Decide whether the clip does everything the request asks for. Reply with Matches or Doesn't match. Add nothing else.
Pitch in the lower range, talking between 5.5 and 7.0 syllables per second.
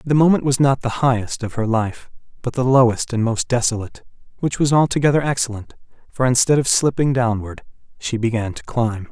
Matches